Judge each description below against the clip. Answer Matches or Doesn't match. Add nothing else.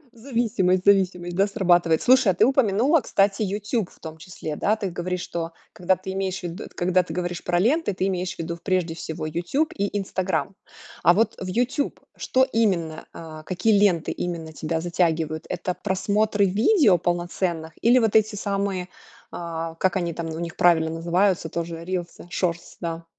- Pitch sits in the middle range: Matches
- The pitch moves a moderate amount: Matches